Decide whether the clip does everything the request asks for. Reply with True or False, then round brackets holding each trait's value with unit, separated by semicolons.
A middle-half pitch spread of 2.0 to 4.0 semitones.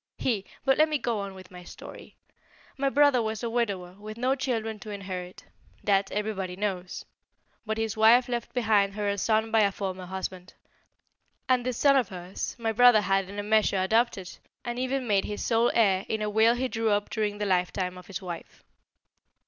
True (3.5 semitones)